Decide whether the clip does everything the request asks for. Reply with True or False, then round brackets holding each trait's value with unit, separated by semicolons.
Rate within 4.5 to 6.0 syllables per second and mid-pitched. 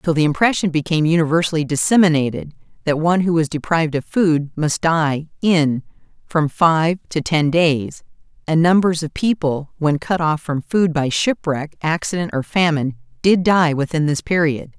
True (5.0 syllables/s; 160 Hz)